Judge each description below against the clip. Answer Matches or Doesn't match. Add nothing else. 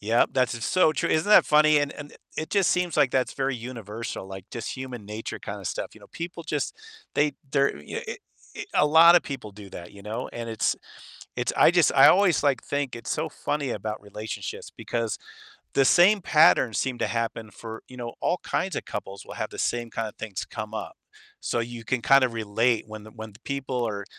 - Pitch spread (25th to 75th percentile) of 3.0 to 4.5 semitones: Doesn't match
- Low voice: Matches